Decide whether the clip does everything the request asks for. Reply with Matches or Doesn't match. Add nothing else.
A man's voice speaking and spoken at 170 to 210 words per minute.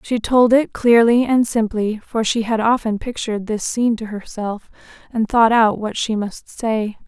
Doesn't match